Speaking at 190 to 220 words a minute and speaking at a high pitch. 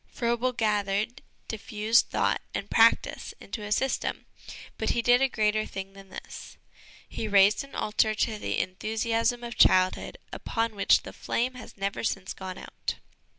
No: average, 155 wpm; high, 215 Hz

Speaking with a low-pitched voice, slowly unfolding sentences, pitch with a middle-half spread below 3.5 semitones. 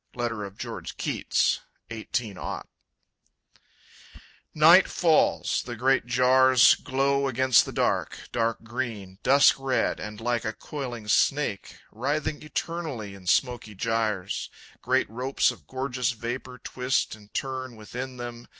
Yes: low, 125 Hz; slow, 125 wpm; average, 2.9 semitones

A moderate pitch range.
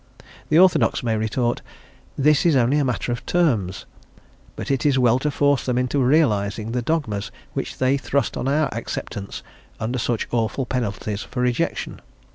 Yes: average, 3.8 semitones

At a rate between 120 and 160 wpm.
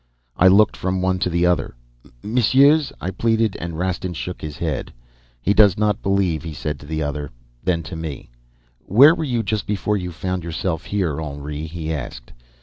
No: average, 185 wpm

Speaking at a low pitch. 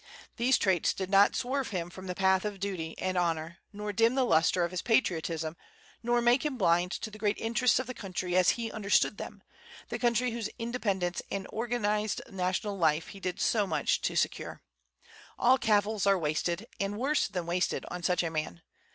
No: high, 195 Hz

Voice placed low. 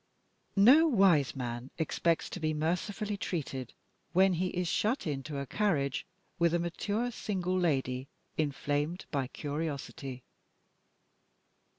No: medium, 165 Hz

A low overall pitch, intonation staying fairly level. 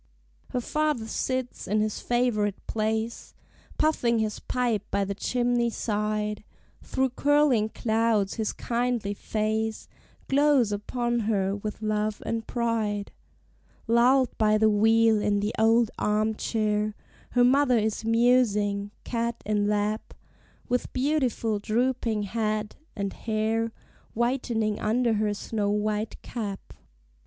No: high, 220 Hz; narrow, 2.3 semitones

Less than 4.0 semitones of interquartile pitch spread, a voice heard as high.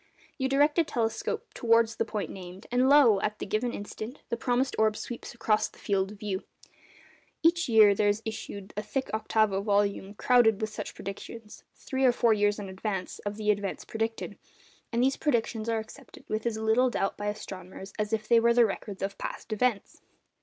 Yes: narrow, 2.5 semitones; high, 220 Hz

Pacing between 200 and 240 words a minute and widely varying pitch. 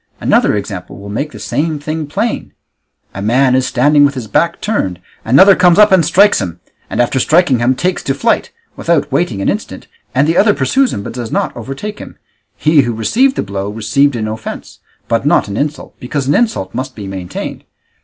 Yes: fast, 205 wpm; wide, 7.1 semitones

